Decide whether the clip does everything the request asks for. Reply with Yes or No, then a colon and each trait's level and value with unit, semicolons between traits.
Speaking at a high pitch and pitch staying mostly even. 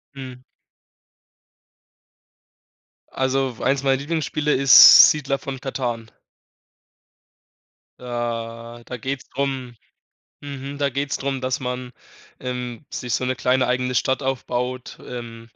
No: low, 130 Hz; narrow, 1.7 semitones